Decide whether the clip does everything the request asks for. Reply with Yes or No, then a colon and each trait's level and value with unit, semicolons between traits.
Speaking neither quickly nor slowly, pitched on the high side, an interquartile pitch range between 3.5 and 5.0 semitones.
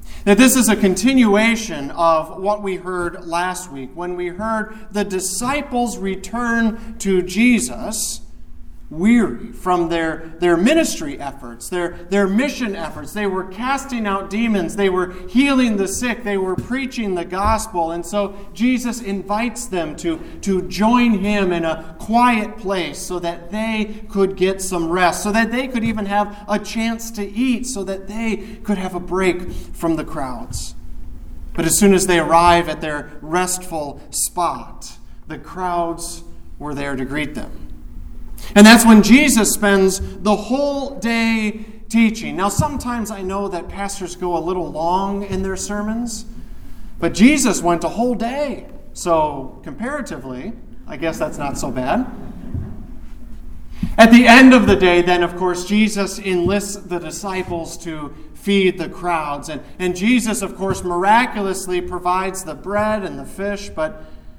Yes: average, 155 wpm; high, 195 Hz; average, 4.2 semitones